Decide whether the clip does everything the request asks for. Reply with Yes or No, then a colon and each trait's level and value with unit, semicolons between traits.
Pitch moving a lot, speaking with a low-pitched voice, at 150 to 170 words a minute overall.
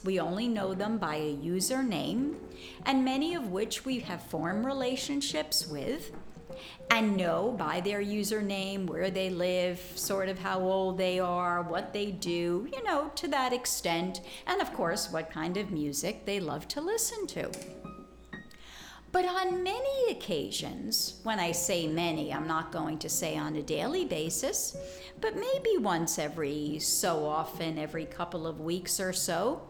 No: wide, 6.2 semitones; medium, 185 Hz; average, 160 wpm